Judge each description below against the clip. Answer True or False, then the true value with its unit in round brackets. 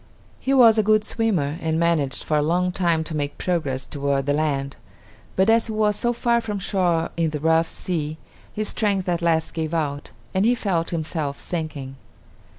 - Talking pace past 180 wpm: True (190 wpm)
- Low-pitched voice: False (165 Hz)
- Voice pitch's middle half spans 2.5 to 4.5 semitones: False (5.0 semitones)